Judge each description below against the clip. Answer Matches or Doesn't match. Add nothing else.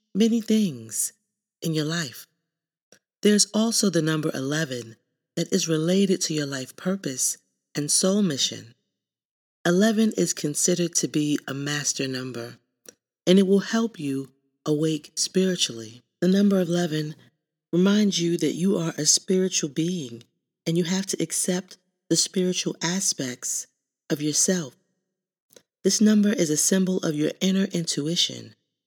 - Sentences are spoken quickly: Doesn't match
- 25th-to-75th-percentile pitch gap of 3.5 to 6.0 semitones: Matches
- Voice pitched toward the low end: Doesn't match